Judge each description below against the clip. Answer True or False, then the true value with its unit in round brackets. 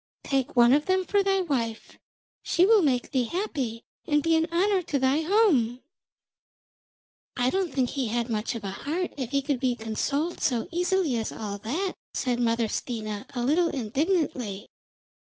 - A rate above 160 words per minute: True (170 wpm)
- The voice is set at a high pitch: True (270 Hz)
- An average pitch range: False (6.4 semitones)